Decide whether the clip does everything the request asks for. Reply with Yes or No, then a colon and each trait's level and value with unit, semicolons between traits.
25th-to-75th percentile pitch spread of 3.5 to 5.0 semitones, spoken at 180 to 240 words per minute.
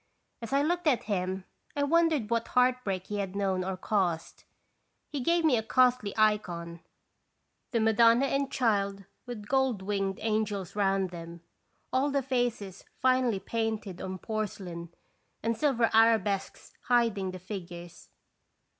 No: average, 4.6 semitones; slow, 135 wpm